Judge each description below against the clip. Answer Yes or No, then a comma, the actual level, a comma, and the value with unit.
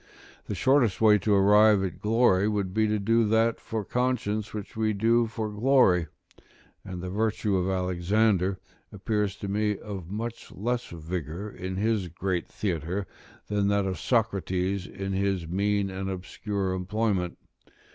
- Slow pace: No, average, 150 wpm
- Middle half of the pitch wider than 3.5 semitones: No, narrow, 2.6 semitones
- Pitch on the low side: Yes, low, 100 Hz